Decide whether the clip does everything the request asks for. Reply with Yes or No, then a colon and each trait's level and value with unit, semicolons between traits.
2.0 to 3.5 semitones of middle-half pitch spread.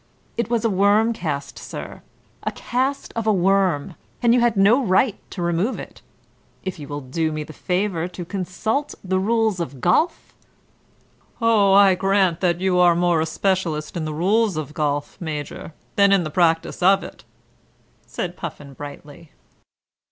No: average, 4.1 semitones